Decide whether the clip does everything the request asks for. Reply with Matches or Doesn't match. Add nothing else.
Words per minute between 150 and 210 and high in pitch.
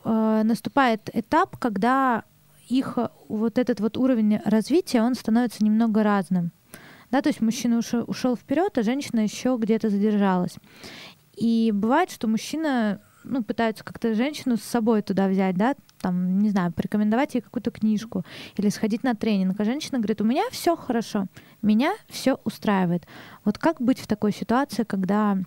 Matches